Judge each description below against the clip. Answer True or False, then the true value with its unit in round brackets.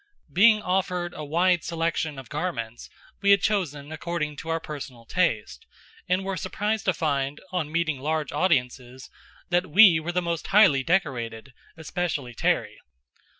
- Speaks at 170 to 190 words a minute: False (150 wpm)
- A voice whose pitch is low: False (165 Hz)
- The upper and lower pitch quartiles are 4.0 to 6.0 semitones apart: True (4.4 semitones)